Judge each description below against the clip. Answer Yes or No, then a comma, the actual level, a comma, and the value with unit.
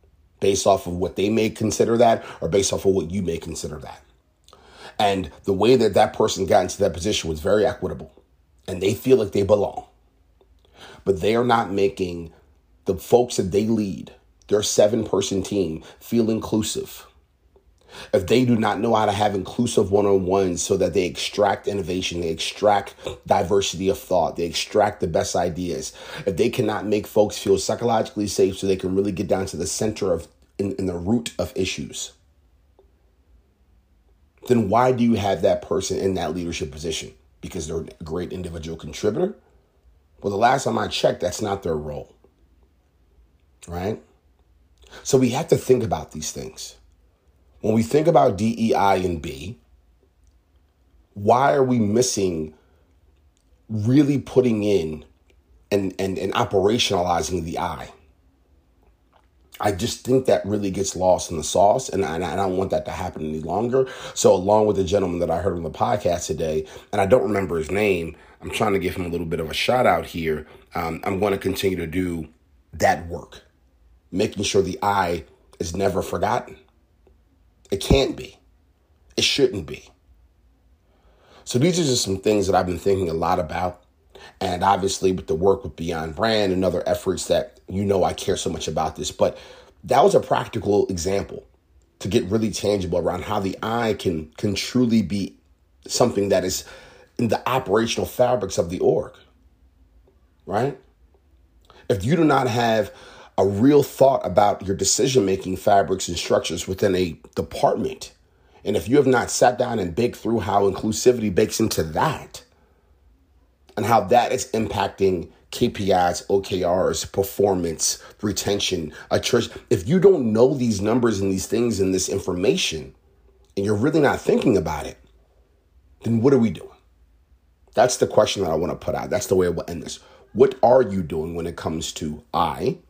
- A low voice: Yes, very low, 95 Hz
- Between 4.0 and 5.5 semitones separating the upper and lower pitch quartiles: Yes, average, 4.6 semitones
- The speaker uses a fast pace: No, average, 175 wpm